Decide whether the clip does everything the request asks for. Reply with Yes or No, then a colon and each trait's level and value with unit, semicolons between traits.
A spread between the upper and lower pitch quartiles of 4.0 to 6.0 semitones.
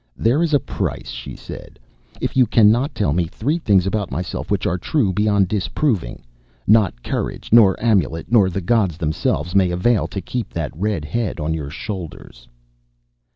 Yes: average, 5.1 semitones